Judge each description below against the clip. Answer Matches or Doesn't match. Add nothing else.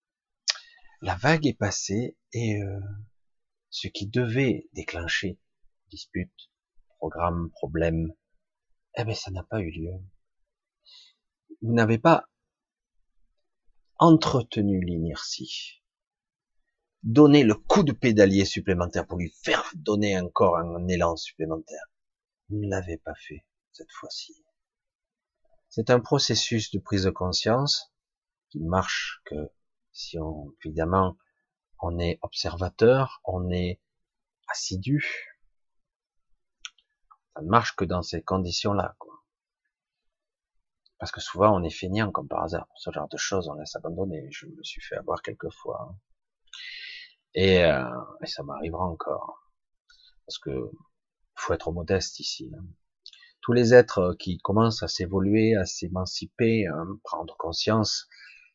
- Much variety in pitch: Matches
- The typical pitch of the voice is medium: Doesn't match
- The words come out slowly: Matches